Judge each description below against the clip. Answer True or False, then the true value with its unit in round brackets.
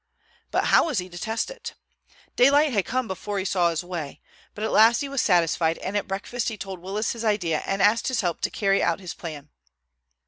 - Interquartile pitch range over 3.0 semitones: True (4.6 semitones)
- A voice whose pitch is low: False (195 Hz)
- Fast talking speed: True (220 wpm)